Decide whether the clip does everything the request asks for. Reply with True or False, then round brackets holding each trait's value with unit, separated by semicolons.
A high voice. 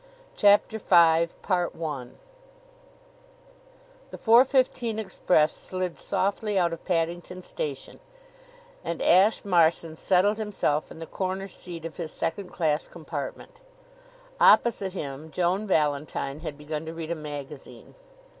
False (180 Hz)